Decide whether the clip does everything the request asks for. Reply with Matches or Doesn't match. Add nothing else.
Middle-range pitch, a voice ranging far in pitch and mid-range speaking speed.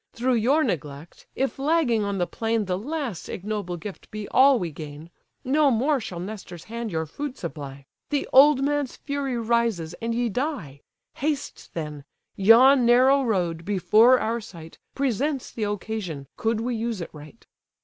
Doesn't match